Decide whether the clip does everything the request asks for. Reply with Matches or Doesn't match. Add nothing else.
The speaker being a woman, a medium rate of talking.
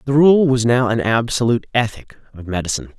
Doesn't match